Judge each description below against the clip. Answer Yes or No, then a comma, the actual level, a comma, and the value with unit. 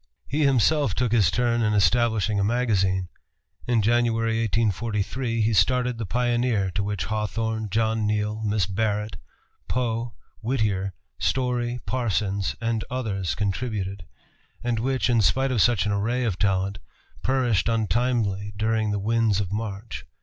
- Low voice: Yes, low, 110 Hz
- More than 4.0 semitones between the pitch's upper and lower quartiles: No, average, 2.9 semitones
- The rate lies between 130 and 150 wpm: Yes, average, 140 wpm